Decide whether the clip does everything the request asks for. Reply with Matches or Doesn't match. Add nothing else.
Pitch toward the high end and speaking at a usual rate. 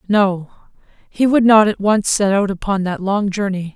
Matches